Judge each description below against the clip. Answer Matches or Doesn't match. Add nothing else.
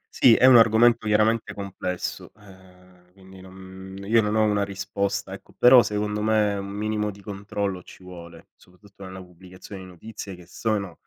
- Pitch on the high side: Doesn't match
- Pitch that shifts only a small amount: Matches